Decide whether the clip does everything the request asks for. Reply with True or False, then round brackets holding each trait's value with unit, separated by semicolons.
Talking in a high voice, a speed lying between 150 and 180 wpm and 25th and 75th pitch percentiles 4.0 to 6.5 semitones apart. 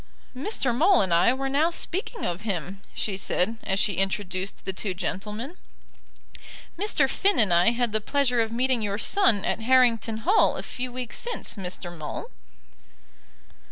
True (230 Hz; 160 wpm; 5.5 semitones)